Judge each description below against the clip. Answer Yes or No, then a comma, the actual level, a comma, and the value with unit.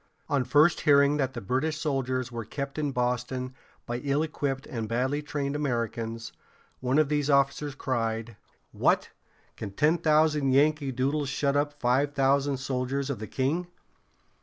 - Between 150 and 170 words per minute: Yes, average, 155 wpm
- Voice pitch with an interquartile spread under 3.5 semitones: Yes, narrow, 2.5 semitones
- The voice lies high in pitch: No, medium, 140 Hz